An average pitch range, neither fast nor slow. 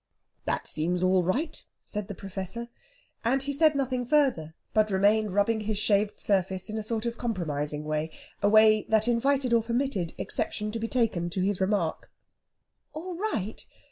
Yes: average, 4.1 semitones; average, 170 wpm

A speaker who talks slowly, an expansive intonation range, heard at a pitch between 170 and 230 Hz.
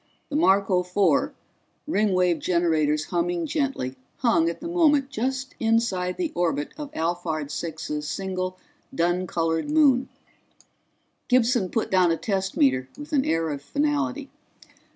Yes: slow, 130 wpm; wide, 8.3 semitones; medium, 185 Hz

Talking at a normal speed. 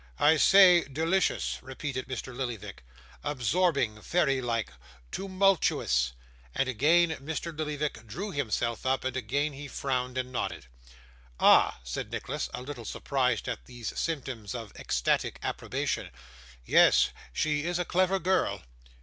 No: slow, 130 wpm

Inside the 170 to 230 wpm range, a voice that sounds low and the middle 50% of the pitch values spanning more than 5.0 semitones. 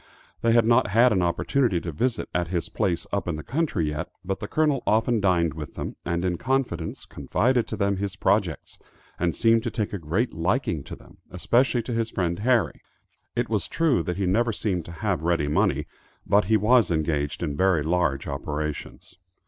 Yes: average, 195 wpm; very low, 95 Hz; wide, 5.4 semitones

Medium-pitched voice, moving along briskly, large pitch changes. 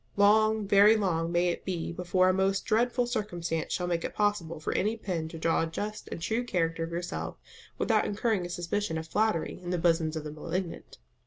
No: medium, 180 Hz; fast, 210 wpm; average, 3.9 semitones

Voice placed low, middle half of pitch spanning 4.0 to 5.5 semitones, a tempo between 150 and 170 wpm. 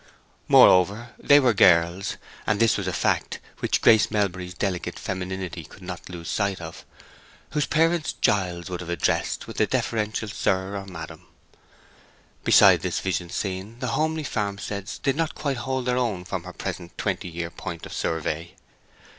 Yes: very low, 95 Hz; average, 4.4 semitones; average, 155 wpm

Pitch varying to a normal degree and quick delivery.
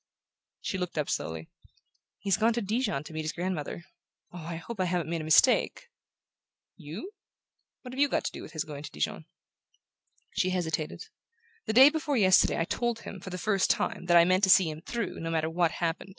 Yes: average, 4.9 semitones; fast, 210 wpm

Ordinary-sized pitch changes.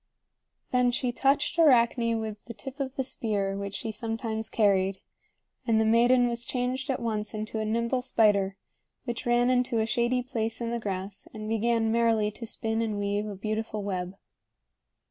No: narrow, 2.3 semitones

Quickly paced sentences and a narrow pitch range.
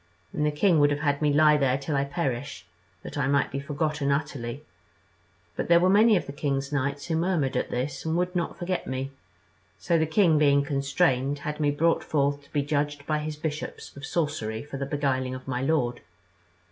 Yes: fast, 210 wpm; narrow, 2.1 semitones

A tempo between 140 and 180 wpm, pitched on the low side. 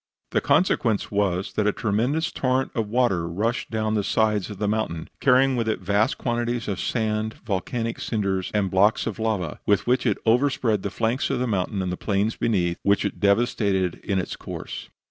No: average, 190 wpm; low, 110 Hz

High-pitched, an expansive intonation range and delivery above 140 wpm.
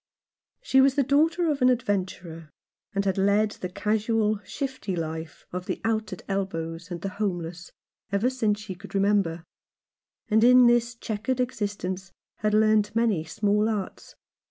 No: high, 210 Hz; average, 3.8 semitones; average, 155 wpm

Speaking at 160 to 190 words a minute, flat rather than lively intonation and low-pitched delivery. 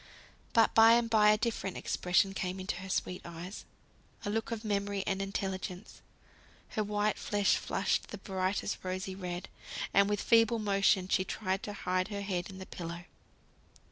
No: average, 170 wpm; narrow, 2.1 semitones; high, 195 Hz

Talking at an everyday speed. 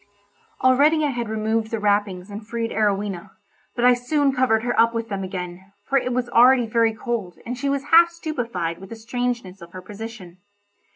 Yes: average, 190 wpm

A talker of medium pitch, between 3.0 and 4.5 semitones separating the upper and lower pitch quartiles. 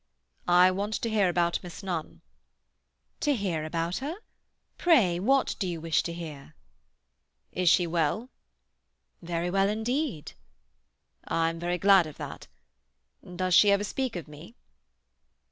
Yes: medium, 180 Hz; average, 3.8 semitones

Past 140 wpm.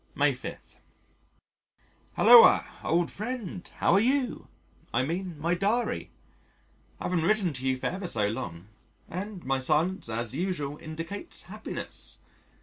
No: slow, 135 wpm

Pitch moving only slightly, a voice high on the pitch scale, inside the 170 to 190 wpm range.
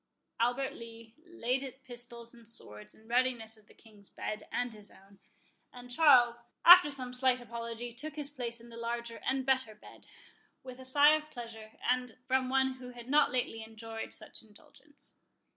Yes: narrow, 2.3 semitones; high, 240 Hz; average, 175 wpm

